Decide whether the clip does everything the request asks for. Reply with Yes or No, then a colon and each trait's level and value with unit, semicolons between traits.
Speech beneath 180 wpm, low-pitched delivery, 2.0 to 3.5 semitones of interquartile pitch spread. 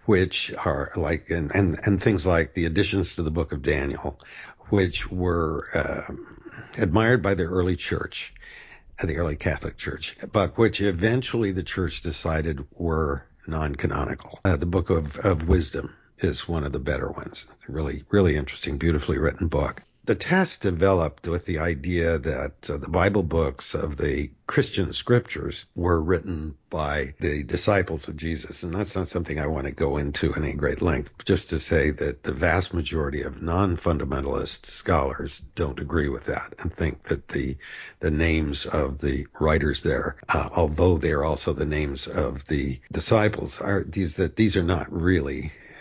No: average, 170 wpm; very low, 85 Hz; average, 3.9 semitones